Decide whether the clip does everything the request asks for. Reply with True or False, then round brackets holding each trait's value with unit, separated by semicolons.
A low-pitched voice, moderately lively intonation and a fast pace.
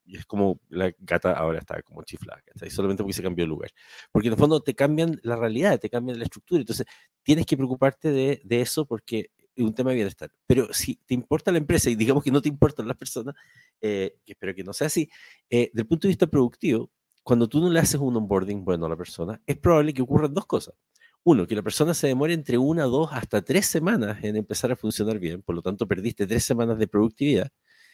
False (120 Hz; 5.9 semitones; 235 wpm)